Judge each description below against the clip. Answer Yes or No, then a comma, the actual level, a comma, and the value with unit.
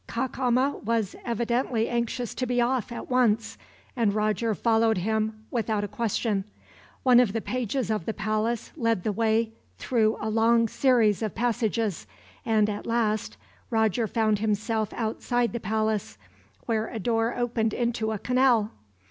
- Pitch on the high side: Yes, high, 225 Hz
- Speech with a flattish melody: Yes, narrow, 1.7 semitones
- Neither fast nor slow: Yes, average, 150 wpm